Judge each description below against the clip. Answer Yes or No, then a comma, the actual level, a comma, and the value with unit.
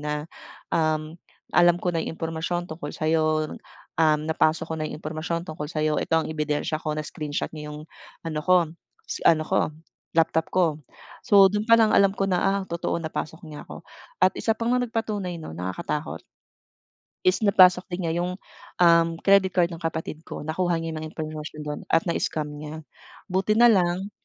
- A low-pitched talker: No, medium, 165 Hz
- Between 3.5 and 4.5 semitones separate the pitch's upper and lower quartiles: No, average, 2.8 semitones